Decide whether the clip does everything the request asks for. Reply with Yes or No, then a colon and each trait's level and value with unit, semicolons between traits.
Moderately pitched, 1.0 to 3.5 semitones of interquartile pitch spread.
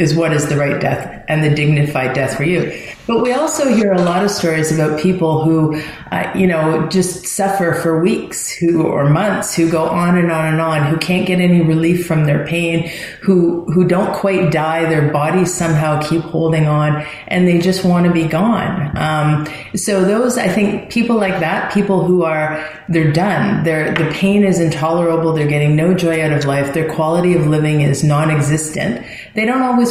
Yes: medium, 165 Hz; average, 3.2 semitones